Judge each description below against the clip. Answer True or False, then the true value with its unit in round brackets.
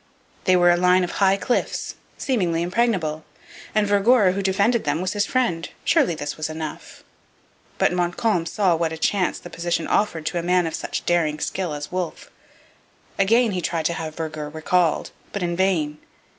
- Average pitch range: True (3.2 semitones)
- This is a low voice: False (175 Hz)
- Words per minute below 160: False (180 wpm)